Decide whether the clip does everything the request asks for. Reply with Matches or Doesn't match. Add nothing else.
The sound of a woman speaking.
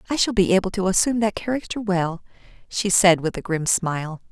Matches